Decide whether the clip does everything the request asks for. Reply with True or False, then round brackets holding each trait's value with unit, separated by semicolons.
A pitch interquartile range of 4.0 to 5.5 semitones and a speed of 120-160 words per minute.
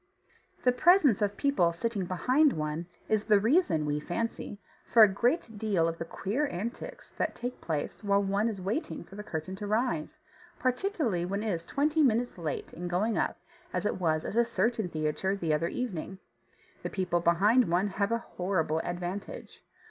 False (5.2 semitones; 180 wpm)